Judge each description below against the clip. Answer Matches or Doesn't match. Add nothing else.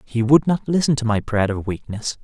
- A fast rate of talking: Matches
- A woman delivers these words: Doesn't match